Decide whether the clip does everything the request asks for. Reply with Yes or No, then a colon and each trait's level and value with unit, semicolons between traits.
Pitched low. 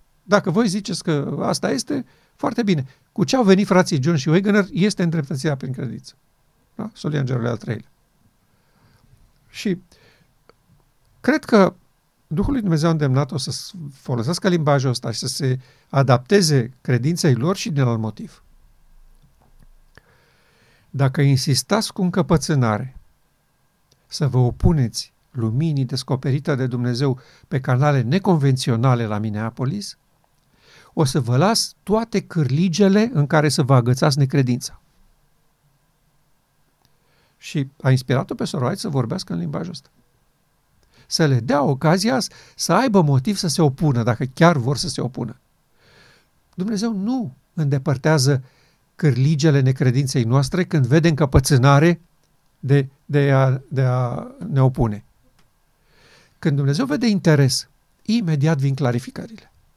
No: medium, 145 Hz